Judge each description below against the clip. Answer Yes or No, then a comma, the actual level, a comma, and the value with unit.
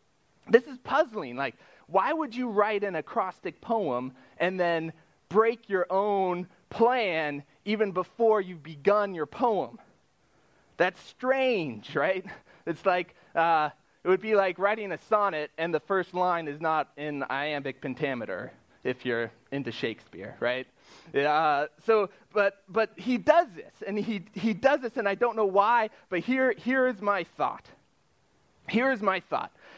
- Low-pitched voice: No, high, 195 Hz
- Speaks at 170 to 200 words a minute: No, average, 155 wpm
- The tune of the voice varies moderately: No, wide, 6.0 semitones